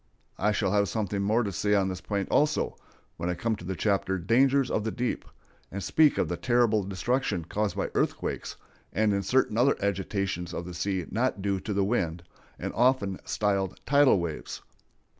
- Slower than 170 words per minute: No, average, 190 wpm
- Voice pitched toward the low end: Yes, low, 100 Hz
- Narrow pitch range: No, average, 3.5 semitones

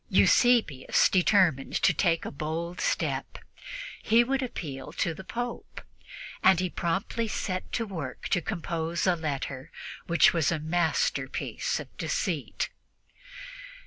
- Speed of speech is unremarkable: No, slow, 125 wpm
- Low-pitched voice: No, medium, 175 Hz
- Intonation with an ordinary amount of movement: Yes, average, 4.3 semitones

